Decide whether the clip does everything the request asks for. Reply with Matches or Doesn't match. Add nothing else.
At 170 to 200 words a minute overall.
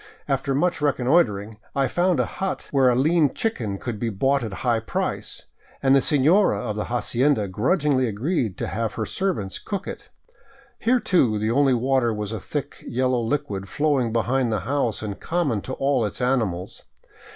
Matches